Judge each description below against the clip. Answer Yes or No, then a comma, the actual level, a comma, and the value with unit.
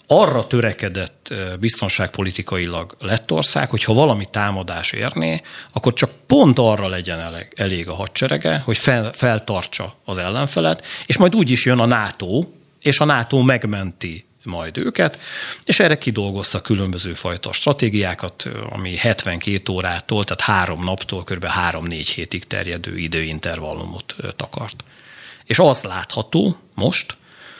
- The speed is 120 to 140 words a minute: Yes, average, 125 wpm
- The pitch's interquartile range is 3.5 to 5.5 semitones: Yes, average, 4.7 semitones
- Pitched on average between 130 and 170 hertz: No, low, 100 Hz